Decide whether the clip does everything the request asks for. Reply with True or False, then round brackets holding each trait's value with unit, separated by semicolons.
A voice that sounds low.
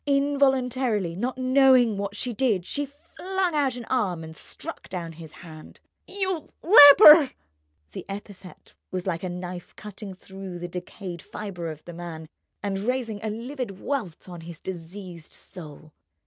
False (200 Hz)